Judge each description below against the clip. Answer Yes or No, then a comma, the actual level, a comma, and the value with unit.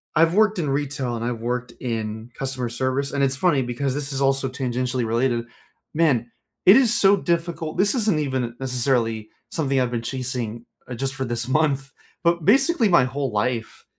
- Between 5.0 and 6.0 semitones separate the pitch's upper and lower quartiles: No, average, 4.3 semitones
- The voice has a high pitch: No, low, 130 Hz